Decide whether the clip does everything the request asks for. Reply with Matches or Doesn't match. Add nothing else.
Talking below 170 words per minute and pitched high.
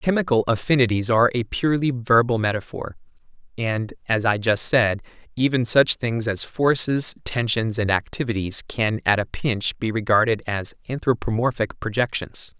Doesn't match